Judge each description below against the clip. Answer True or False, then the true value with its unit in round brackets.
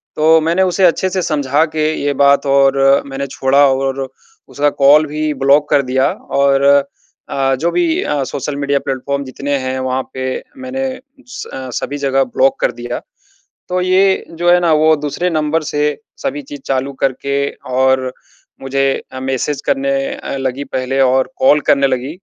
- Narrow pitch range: False (3.2 semitones)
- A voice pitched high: False (140 Hz)